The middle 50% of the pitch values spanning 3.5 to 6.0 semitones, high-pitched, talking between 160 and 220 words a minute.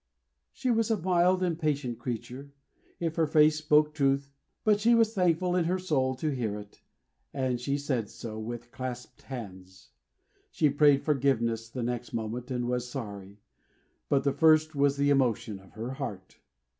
No: average, 4.7 semitones; low, 135 Hz; average, 170 wpm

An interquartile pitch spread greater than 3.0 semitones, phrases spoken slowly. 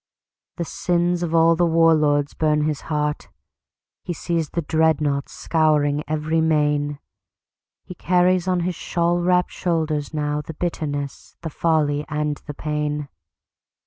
No: narrow, 2.4 semitones; slow, 125 wpm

